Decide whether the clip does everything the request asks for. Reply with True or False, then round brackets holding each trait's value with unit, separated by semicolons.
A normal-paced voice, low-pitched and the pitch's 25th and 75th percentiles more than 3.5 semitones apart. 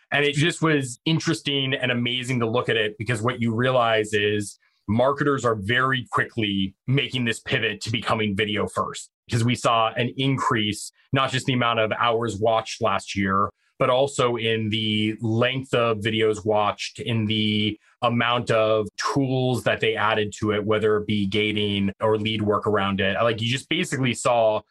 False (175 wpm; 115 Hz; 2.9 semitones)